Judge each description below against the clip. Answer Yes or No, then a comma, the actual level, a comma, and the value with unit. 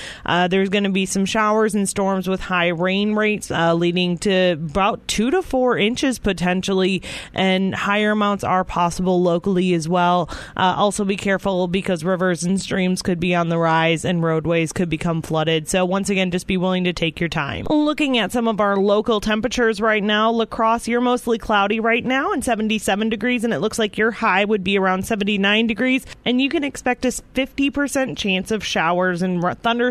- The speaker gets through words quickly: No, average, 195 wpm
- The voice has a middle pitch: No, high, 195 Hz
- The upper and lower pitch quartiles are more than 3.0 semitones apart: Yes, average, 3.7 semitones